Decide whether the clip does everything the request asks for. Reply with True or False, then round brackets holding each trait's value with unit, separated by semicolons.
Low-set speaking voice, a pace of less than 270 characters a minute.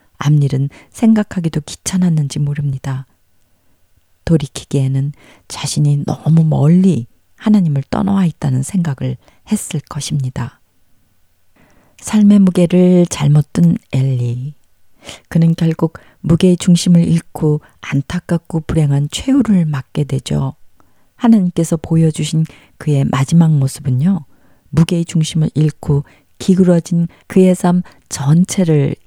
False (155 Hz; 250 characters per minute)